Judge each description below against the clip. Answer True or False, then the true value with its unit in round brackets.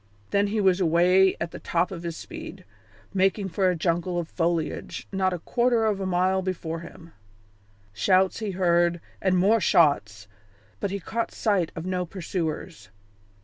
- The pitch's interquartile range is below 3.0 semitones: True (2.4 semitones)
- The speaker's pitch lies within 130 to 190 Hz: True (185 Hz)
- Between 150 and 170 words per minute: True (165 wpm)